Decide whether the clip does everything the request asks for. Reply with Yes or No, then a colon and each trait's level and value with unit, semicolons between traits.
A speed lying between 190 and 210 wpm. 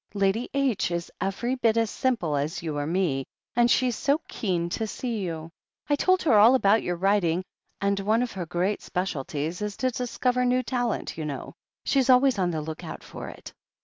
Yes: average, 200 wpm